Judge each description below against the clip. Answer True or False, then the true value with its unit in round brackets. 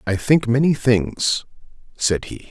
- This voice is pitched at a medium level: False (120 Hz)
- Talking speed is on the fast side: False (145 wpm)